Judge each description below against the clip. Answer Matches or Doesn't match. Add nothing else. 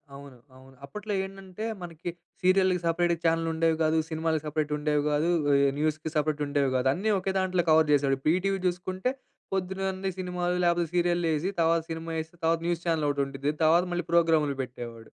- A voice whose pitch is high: Doesn't match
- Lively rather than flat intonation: Doesn't match